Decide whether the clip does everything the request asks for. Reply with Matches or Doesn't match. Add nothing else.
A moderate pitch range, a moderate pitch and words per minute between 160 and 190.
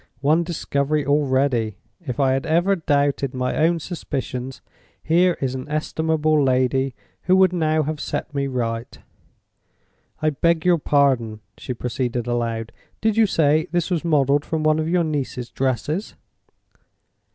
Doesn't match